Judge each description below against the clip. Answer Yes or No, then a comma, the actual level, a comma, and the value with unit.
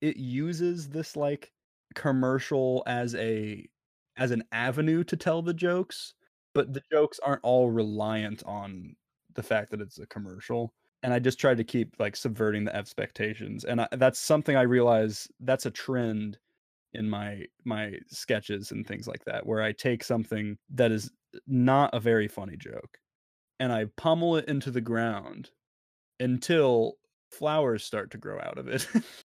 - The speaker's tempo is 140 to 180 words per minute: Yes, average, 165 wpm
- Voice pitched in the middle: No, low, 125 Hz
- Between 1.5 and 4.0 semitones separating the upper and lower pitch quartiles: No, average, 4.4 semitones